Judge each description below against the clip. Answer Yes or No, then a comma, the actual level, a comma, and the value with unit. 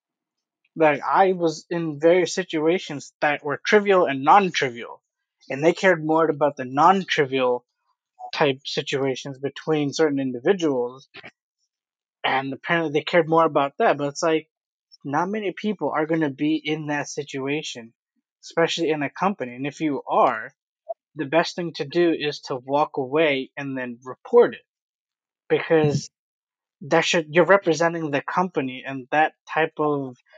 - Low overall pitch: No, medium, 155 Hz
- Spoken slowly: No, average, 150 wpm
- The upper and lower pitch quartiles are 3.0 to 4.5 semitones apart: Yes, average, 3.4 semitones